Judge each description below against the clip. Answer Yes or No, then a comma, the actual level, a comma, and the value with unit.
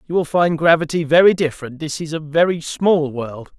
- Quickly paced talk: No, average, 185 wpm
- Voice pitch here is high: No, medium, 155 Hz